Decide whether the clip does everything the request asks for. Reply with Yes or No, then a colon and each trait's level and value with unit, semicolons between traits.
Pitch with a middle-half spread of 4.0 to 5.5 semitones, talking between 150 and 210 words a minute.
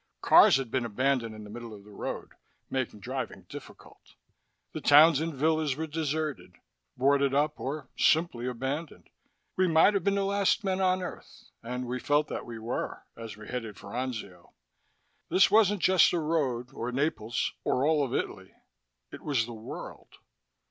Yes: average, 5.2 semitones; average, 170 wpm